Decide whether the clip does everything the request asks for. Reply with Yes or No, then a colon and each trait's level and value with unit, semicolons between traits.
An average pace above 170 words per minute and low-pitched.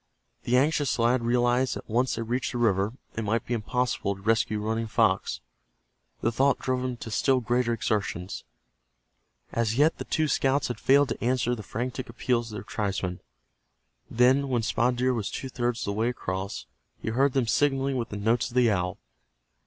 Yes: average, 190 wpm; low, 120 Hz